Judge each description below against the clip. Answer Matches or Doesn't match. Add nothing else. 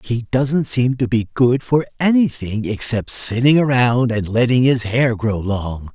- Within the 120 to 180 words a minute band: Matches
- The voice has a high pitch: Doesn't match